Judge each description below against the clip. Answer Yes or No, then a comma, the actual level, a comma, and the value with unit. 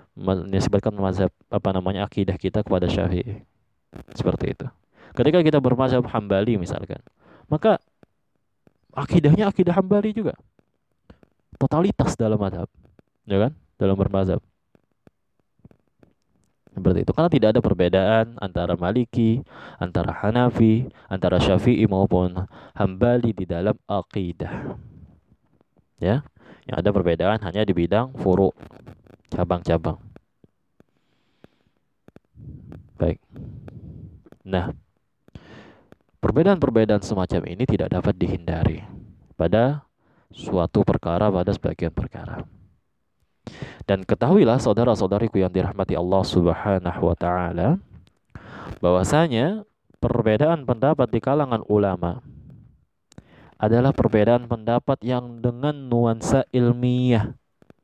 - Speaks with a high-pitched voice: No, low, 105 Hz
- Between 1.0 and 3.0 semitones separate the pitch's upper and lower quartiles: No, average, 4.7 semitones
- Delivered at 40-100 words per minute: Yes, average, 90 wpm